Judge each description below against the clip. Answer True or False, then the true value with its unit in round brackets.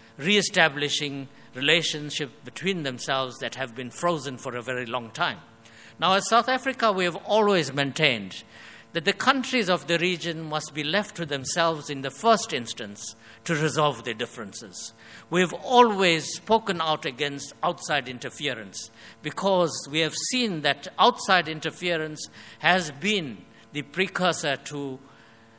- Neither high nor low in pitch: True (155 Hz)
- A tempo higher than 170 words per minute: False (140 wpm)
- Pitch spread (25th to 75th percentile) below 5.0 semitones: False (5.3 semitones)